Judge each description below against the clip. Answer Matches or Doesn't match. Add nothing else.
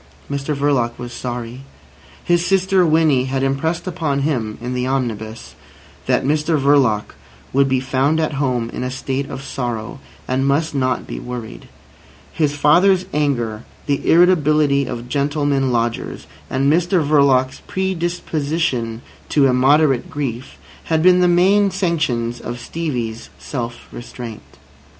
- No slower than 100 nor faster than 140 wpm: Matches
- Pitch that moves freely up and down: Doesn't match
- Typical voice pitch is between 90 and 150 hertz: Matches